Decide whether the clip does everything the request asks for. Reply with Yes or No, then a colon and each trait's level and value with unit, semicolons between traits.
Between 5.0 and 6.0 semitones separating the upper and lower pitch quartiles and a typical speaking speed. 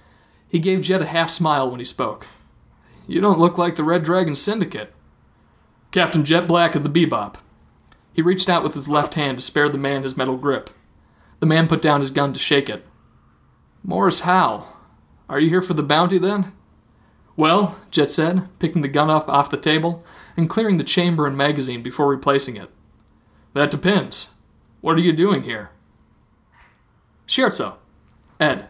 No: average, 3.9 semitones; average, 175 wpm